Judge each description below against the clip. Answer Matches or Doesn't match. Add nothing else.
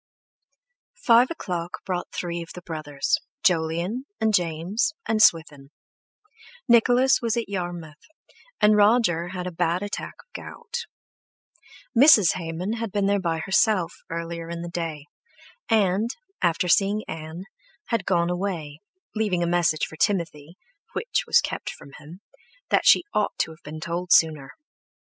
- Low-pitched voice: Doesn't match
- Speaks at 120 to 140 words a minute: Matches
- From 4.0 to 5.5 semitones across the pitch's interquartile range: Matches